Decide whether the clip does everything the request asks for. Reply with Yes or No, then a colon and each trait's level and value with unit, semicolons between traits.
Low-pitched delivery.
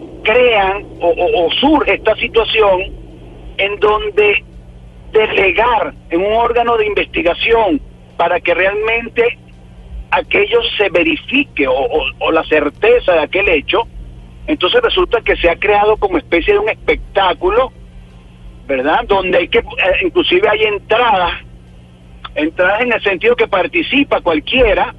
No: high, 210 Hz